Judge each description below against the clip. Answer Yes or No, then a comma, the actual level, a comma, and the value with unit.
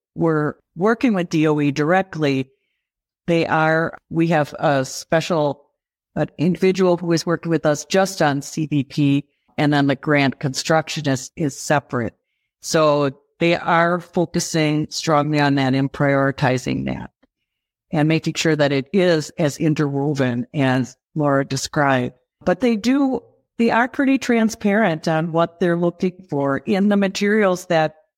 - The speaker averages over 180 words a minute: No, average, 140 wpm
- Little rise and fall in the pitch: No, average, 3.6 semitones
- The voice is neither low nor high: Yes, medium, 155 Hz